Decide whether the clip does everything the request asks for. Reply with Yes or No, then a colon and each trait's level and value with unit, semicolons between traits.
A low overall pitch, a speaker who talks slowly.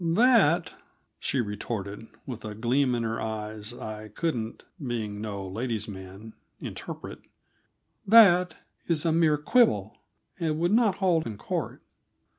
Yes: low, 120 Hz; slow, 130 wpm